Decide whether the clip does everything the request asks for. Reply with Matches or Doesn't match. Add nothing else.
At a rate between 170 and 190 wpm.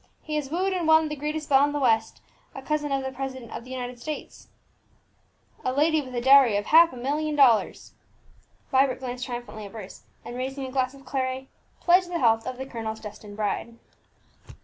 Doesn't match